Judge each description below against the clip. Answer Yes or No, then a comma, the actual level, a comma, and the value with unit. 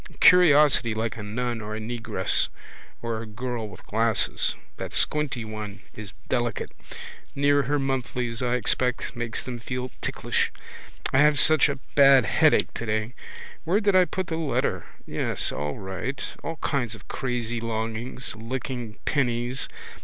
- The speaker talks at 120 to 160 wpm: Yes, average, 145 wpm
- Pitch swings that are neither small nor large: Yes, average, 3.5 semitones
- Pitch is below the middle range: Yes, low, 120 Hz